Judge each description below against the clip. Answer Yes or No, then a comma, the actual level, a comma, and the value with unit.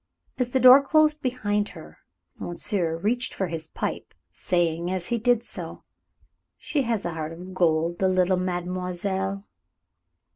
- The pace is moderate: Yes, average, 145 wpm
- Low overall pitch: No, medium, 185 Hz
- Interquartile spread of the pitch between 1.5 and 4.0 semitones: No, average, 5.3 semitones